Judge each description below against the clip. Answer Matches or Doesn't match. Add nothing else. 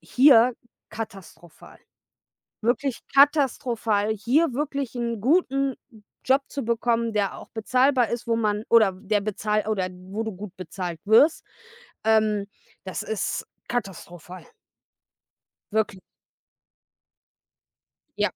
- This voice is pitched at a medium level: Doesn't match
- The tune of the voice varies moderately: Matches